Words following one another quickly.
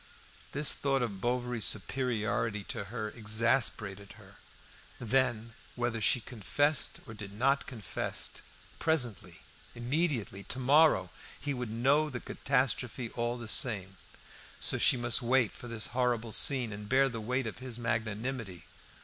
No: average, 140 wpm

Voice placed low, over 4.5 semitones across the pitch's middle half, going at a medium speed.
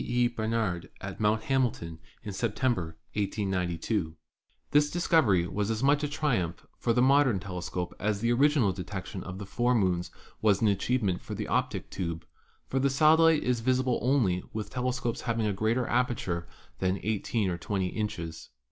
Yes: low, 110 Hz; average, 5.3 semitones; average, 170 wpm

